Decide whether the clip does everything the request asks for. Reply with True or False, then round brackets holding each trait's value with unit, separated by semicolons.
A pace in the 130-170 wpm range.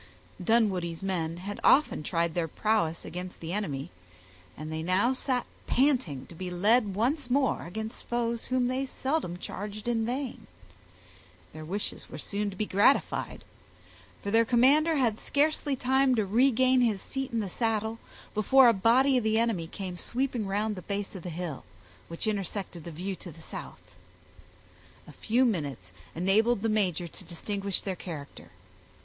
True (165 wpm)